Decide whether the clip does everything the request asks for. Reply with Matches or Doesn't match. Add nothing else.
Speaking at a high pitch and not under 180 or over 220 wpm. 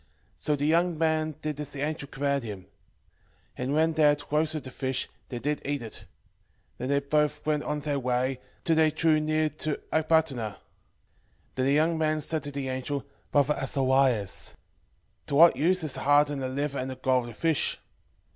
Doesn't match